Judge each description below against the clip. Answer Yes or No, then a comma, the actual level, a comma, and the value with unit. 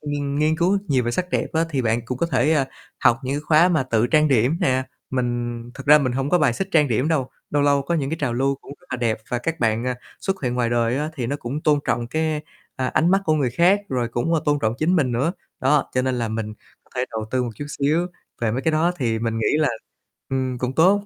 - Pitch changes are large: No, average, 4.3 semitones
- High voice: No, low, 135 Hz